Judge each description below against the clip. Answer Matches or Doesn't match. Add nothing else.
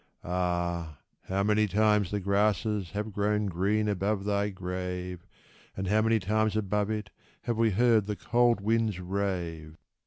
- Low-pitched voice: Matches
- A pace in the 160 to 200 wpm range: Doesn't match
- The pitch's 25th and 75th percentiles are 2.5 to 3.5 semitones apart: Matches